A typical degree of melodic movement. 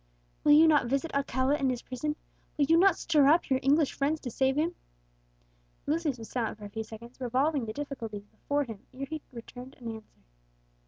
Yes: average, 3.9 semitones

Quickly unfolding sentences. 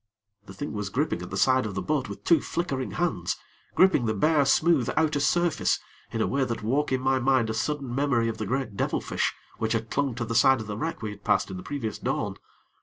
Yes: fast, 240 wpm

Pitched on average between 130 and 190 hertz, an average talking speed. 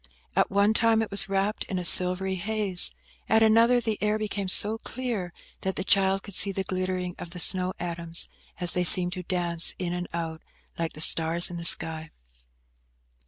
Yes: medium, 185 Hz; average, 190 wpm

